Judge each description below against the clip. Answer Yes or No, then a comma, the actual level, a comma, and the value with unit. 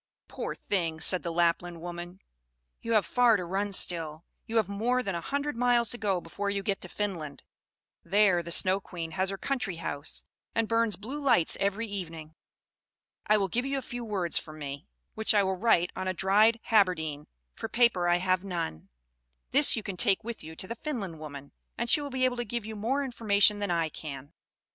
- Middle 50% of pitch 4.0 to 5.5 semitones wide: Yes, average, 5.0 semitones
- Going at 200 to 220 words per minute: Yes, fast, 205 wpm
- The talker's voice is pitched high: Yes, high, 195 Hz